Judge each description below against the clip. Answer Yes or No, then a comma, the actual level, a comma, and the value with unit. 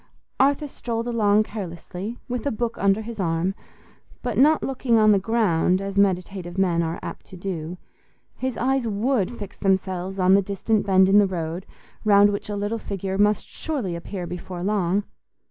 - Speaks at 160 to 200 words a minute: Yes, average, 175 wpm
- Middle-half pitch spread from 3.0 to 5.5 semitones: Yes, average, 3.5 semitones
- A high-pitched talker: Yes, high, 200 Hz